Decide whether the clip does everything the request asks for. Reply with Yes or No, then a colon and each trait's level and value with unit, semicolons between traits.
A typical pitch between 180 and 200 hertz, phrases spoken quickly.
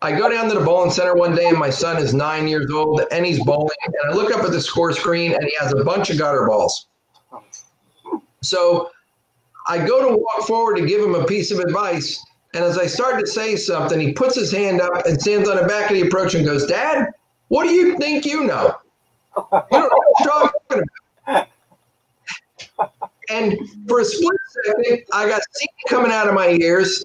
Yes: high, 190 Hz; fast, 210 wpm